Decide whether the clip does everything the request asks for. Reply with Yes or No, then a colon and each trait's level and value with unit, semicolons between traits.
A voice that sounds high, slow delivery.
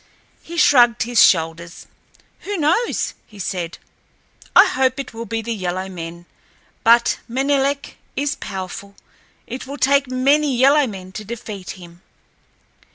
Yes: high, 235 Hz; slow, 130 wpm